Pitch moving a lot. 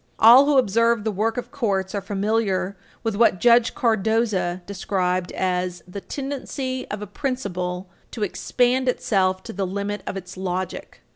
No: average, 3.9 semitones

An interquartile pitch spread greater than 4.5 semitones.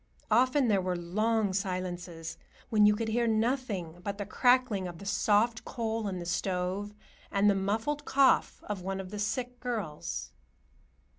No: average, 3.8 semitones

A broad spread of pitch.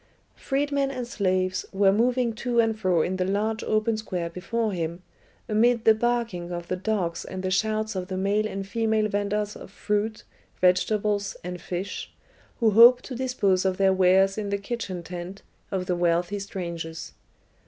No: average, 3.1 semitones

